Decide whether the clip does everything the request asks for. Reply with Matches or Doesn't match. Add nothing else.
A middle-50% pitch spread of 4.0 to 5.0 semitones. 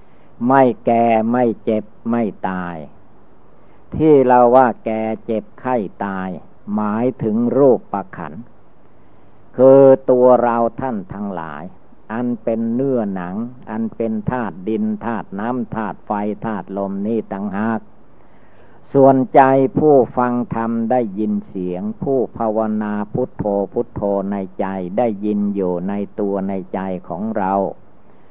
Doesn't match